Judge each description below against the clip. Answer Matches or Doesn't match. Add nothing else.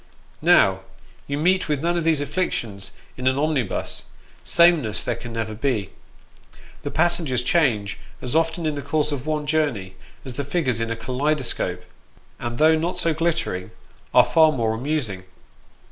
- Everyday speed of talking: Matches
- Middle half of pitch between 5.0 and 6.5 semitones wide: Matches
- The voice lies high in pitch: Doesn't match